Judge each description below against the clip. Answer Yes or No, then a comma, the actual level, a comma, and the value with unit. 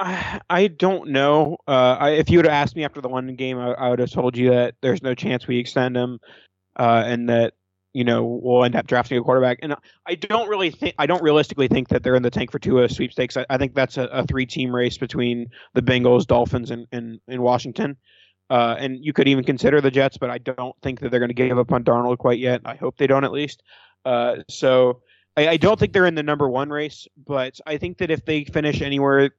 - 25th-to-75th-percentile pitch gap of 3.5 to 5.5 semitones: No, average, 2.8 semitones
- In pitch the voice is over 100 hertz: Yes, low, 130 Hz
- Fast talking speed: Yes, fast, 245 wpm